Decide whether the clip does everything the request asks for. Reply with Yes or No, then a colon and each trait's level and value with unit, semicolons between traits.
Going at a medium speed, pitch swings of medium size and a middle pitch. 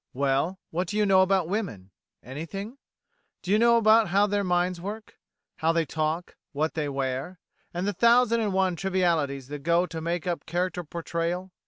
Yes: average, 175 wpm; average, 3.6 semitones; medium, 175 Hz